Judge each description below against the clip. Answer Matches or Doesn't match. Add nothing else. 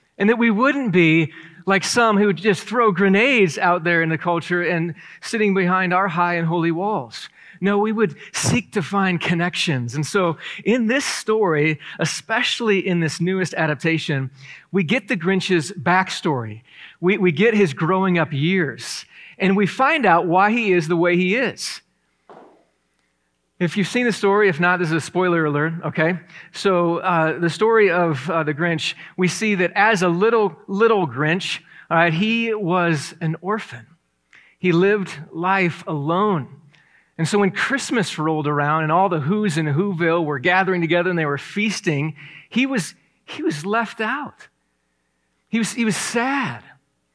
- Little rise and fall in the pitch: Doesn't match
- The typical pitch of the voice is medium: Matches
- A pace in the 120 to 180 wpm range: Matches